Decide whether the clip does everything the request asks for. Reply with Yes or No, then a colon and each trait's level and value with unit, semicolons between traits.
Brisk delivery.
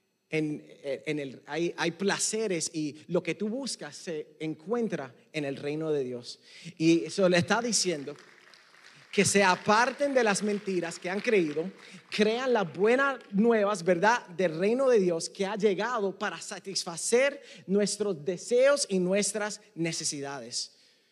No: average, 145 wpm